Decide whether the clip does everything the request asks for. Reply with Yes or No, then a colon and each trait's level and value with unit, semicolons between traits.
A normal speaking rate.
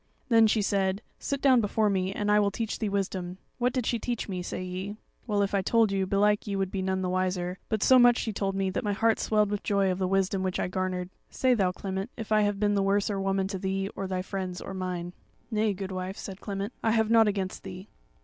No: fast, 250 wpm